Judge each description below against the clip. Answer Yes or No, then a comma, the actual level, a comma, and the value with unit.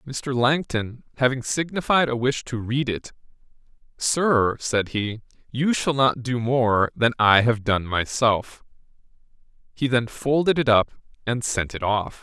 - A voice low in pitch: Yes, low, 125 Hz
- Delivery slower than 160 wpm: Yes, average, 150 wpm